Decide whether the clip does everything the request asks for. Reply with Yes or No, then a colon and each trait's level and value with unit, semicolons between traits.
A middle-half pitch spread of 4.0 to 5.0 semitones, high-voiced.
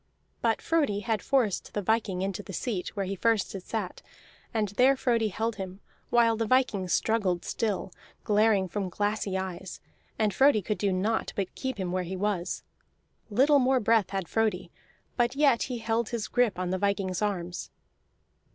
No: average, 3.4 semitones; high, 210 Hz